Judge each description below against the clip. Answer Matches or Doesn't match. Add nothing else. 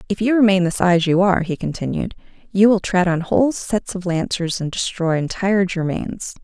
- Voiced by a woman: Matches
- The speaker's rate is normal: Matches